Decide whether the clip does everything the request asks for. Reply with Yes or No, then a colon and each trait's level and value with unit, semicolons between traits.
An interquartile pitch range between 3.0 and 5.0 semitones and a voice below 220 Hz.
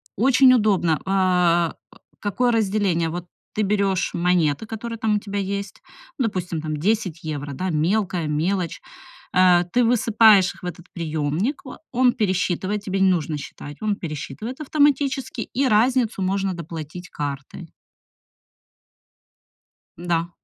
Yes: average, 4.5 semitones; high, 190 Hz